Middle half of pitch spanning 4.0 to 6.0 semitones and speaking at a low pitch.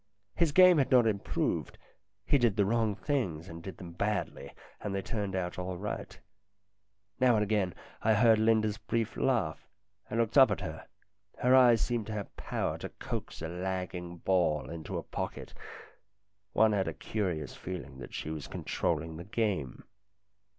Yes: average, 4.4 semitones; low, 105 Hz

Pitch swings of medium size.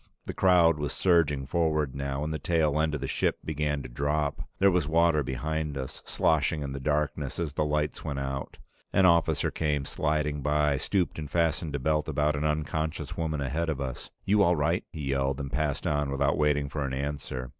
No: narrow, 2.0 semitones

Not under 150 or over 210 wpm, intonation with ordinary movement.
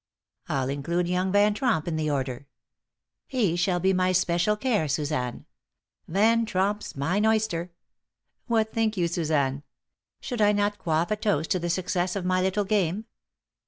Yes: average, 160 wpm; average, 4.4 semitones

